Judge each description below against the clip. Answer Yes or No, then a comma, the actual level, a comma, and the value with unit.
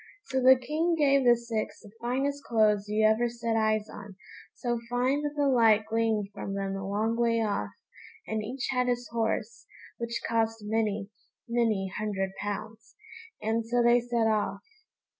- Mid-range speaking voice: No, high, 225 Hz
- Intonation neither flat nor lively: No, narrow, 2.3 semitones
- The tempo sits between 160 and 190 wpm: Yes, average, 165 wpm